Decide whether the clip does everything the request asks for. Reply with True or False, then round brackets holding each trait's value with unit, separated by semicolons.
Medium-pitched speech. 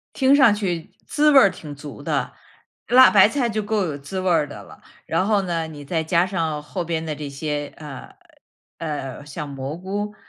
True (165 Hz)